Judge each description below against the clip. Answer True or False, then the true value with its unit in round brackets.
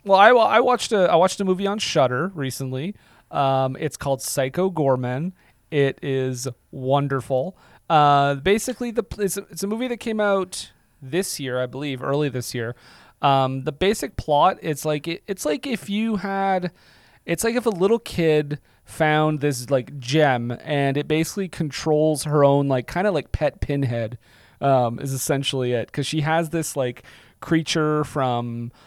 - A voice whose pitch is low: False (150 Hz)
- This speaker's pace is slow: False (175 wpm)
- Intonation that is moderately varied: False (5.8 semitones)